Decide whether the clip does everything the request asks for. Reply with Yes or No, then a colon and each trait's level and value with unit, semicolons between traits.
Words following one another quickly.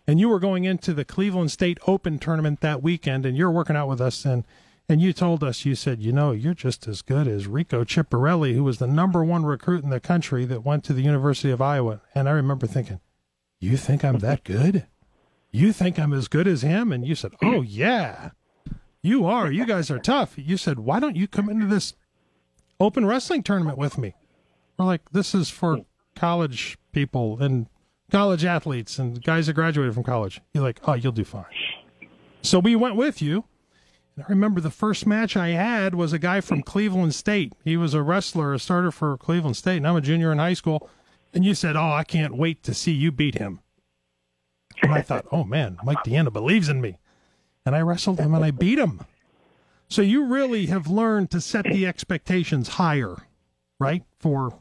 Yes: fast, 210 wpm